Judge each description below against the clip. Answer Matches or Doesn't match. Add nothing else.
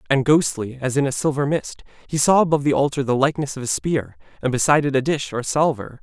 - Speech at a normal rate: Doesn't match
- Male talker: Matches